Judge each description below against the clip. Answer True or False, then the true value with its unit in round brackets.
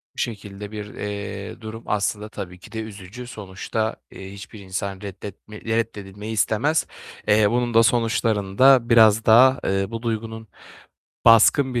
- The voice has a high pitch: False (110 Hz)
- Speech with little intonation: True (2.3 semitones)